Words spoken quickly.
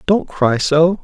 No: average, 175 wpm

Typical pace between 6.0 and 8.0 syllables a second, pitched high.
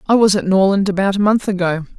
Yes: 6.2 syllables/s; high, 195 Hz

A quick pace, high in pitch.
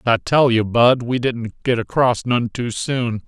No: fast, 220 wpm; low, 120 Hz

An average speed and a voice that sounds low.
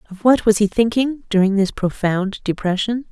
No: average, 175 wpm; high, 210 Hz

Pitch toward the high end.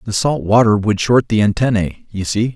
No: low, 110 Hz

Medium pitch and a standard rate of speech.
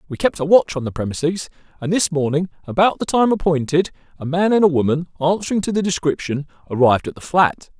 No: medium, 160 Hz; fast, 210 wpm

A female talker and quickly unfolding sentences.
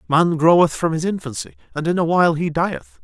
No: male; fast, 220 wpm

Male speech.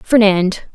No: female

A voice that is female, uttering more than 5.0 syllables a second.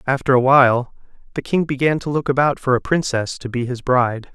No: male; 5.8 syllables/s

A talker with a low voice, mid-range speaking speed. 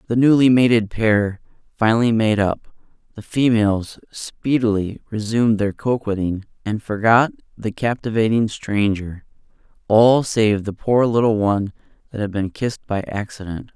No: low, 110 Hz; slow, 125 wpm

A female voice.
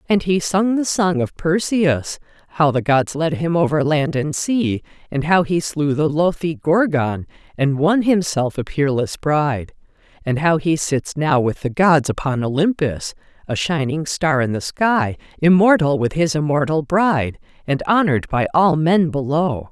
Yes: female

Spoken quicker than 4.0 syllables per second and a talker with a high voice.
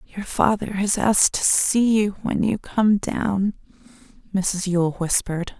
No: 3.9 syllables/s; high, 200 Hz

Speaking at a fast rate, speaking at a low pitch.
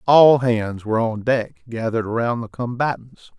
No: average, 160 wpm; low, 120 Hz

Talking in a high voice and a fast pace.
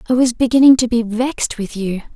Yes: high, 235 Hz; fast, 225 wpm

